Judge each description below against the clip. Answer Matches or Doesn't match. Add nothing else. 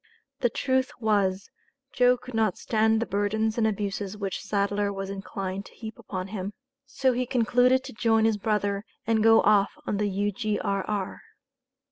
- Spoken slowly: Doesn't match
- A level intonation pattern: Matches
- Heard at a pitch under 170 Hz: Doesn't match